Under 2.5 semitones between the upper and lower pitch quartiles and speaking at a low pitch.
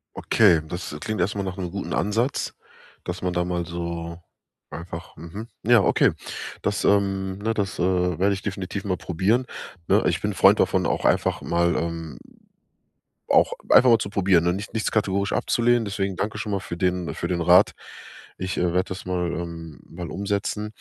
No: average, 2.8 semitones; very low, 95 Hz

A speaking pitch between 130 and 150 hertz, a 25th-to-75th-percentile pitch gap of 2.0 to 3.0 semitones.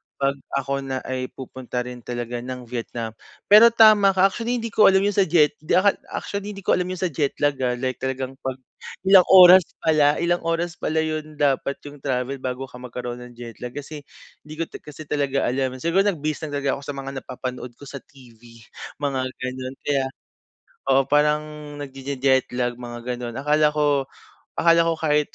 No: medium, 140 Hz; average, 4.1 semitones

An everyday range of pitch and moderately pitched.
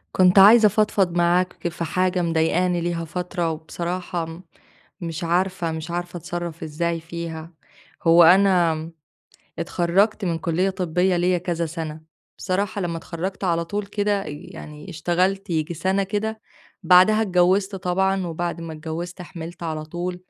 No: narrow, 2.1 semitones; medium, 175 Hz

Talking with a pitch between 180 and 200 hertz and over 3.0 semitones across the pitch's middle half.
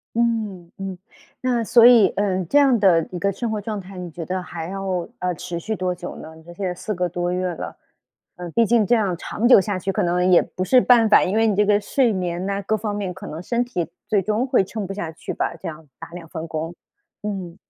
Yes: high, 190 Hz; average, 3.5 semitones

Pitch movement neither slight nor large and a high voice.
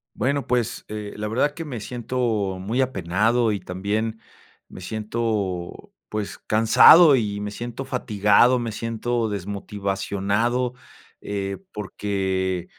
No: average, 3.2 semitones; low, 110 Hz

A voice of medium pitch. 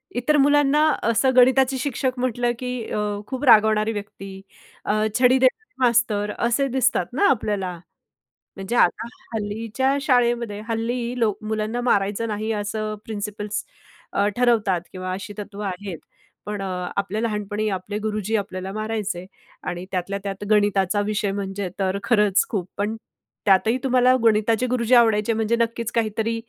No: high, 215 Hz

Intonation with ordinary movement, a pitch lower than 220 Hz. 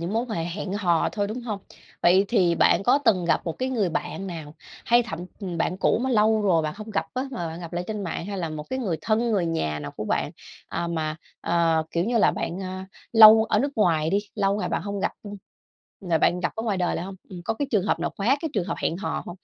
Yes: average, 4.3 semitones; high, 190 Hz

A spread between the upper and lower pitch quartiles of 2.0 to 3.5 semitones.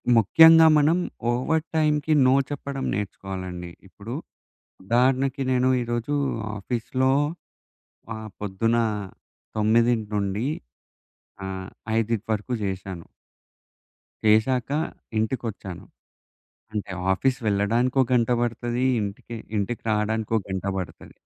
No: average, 4.2 semitones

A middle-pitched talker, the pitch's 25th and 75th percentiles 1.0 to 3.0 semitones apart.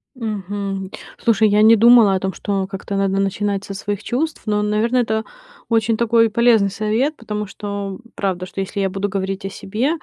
No: high, 205 Hz; narrow, 2.4 semitones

